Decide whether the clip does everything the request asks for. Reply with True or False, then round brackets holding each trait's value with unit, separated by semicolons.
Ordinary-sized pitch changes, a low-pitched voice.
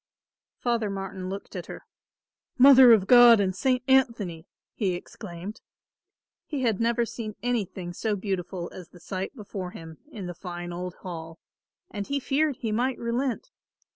False (5.0 semitones; 205 Hz)